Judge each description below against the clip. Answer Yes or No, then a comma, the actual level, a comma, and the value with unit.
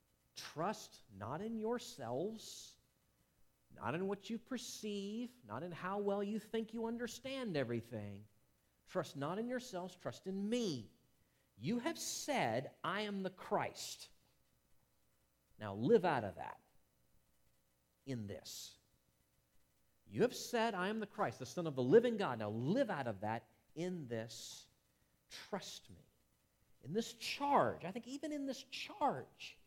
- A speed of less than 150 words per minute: Yes, average, 140 wpm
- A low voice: No, medium, 170 Hz